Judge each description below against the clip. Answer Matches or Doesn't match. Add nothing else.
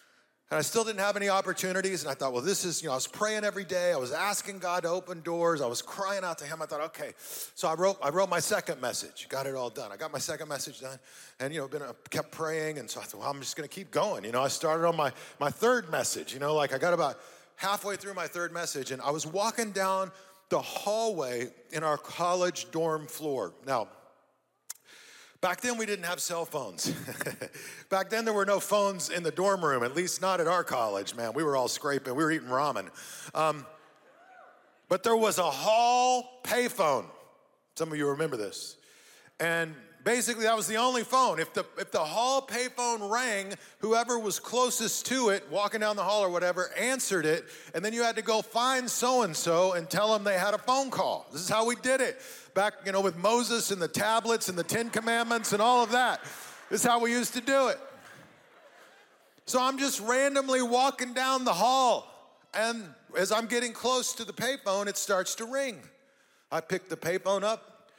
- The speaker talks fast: Matches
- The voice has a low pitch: Doesn't match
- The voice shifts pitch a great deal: Matches